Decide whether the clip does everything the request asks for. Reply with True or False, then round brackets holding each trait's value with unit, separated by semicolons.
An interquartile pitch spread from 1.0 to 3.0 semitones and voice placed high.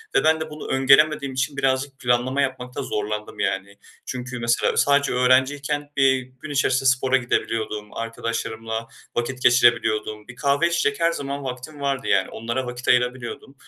False (2.6 semitones; 130 Hz)